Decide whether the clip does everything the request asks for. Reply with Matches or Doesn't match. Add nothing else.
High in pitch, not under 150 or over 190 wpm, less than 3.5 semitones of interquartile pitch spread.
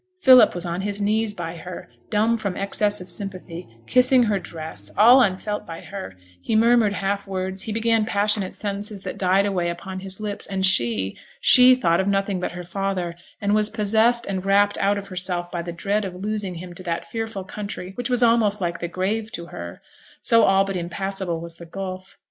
Doesn't match